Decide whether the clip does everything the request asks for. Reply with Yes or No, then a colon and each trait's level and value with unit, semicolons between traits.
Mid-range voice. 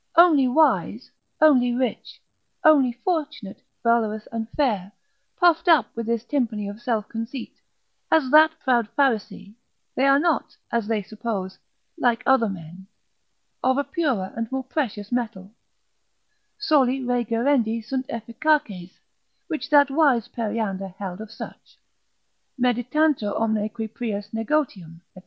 No: high, 235 Hz